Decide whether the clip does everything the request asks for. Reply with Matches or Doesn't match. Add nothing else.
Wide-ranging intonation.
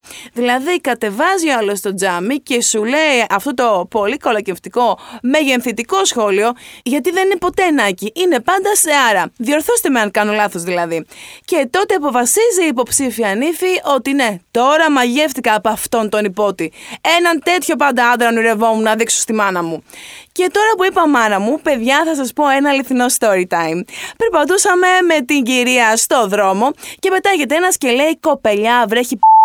Matches